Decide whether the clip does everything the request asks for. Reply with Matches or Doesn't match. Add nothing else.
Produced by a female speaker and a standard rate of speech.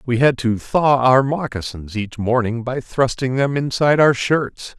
Doesn't match